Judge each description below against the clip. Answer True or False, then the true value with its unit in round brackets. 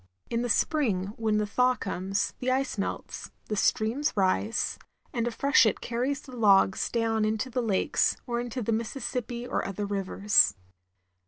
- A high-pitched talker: True (225 Hz)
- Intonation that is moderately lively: True (3.3 semitones)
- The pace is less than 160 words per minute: False (165 wpm)